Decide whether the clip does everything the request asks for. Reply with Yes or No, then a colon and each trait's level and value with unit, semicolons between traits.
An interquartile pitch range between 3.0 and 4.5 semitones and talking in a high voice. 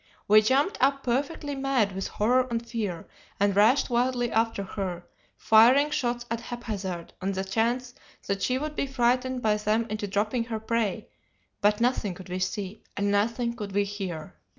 Yes: average, 3.6 semitones; high, 225 Hz